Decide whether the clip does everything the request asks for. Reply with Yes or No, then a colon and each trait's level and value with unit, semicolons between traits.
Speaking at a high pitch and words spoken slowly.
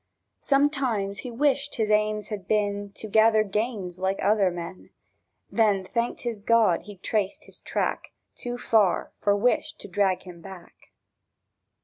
No: high, 210 Hz; average, 145 wpm